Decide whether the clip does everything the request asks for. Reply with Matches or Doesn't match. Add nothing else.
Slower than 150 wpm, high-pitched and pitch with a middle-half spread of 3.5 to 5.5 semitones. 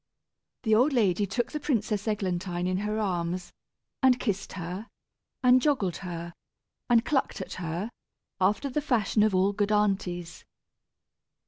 Matches